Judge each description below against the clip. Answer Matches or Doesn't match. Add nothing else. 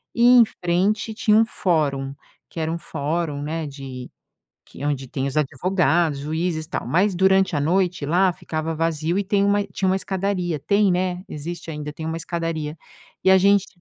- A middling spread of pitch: Matches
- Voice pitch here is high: Doesn't match